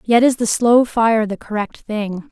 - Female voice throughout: Yes, female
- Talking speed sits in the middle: No, fast, 210 wpm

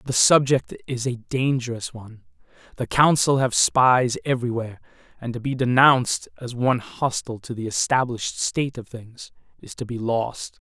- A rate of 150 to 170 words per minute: Yes, average, 160 wpm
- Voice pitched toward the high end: No, low, 125 Hz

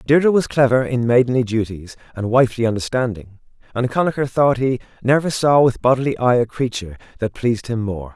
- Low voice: Yes, low, 120 Hz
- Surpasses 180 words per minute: No, average, 175 wpm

